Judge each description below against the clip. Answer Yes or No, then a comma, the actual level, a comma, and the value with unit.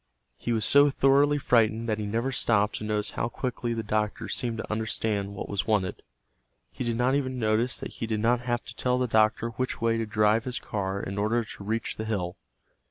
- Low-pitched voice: Yes, low, 115 Hz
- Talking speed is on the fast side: Yes, fast, 220 wpm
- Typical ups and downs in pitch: No, narrow, 2.3 semitones